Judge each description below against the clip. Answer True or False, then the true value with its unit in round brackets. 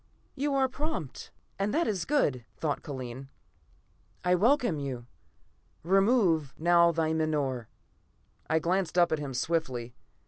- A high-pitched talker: False (165 Hz)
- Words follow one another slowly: True (130 wpm)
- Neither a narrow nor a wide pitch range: False (5.9 semitones)